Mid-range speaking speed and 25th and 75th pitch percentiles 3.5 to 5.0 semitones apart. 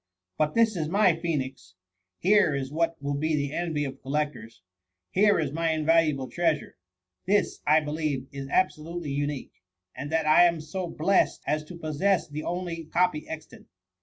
No: average, 180 wpm; average, 3.0 semitones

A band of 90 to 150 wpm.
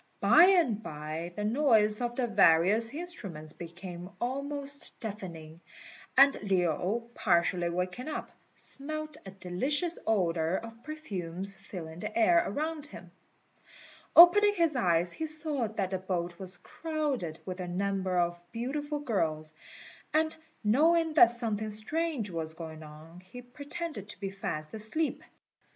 Yes: slow, 135 wpm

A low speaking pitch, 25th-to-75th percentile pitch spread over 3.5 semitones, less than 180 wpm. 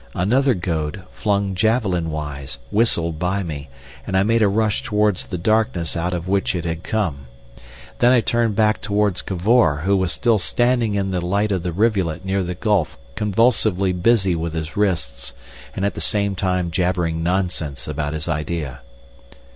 Yes: very low, 95 Hz; average, 4.0 semitones; average, 170 wpm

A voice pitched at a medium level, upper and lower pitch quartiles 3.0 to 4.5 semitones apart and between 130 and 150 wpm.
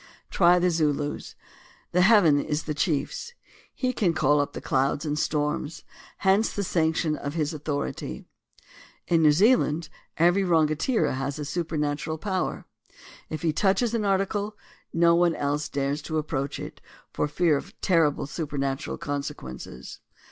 Yes: medium, 155 Hz; average, 3.4 semitones; average, 140 wpm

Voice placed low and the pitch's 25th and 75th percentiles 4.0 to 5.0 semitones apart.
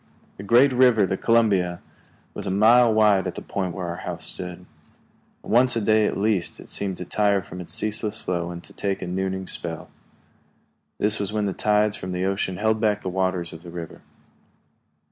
No: low, 100 Hz; average, 3.0 semitones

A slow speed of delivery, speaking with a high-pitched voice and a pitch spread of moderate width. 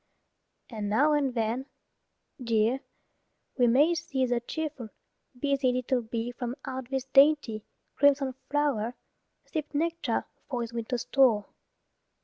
Yes: slow, 125 wpm; very high, 260 Hz; average, 3.4 semitones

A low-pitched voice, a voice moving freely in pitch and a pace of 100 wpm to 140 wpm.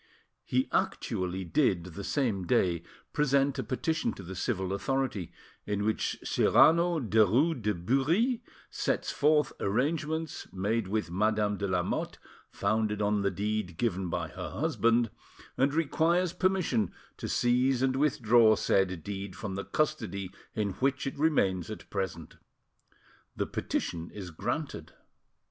Yes: low, 110 Hz; wide, 6.0 semitones; slow, 135 wpm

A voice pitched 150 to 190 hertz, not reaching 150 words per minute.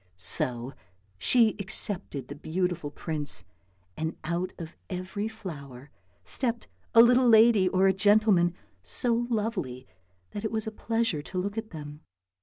Yes: medium, 185 Hz; average, 140 wpm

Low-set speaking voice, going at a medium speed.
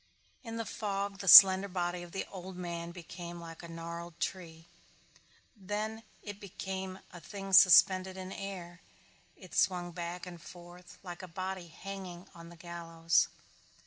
No: medium, 180 Hz; average, 155 wpm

